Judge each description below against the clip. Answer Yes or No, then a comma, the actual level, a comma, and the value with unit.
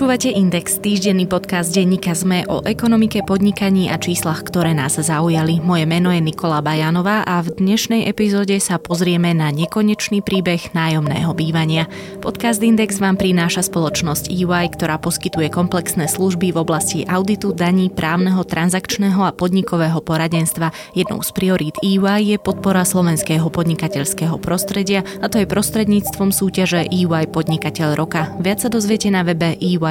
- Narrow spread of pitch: No, average, 3.2 semitones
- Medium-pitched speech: Yes, medium, 180 Hz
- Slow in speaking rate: No, average, 145 wpm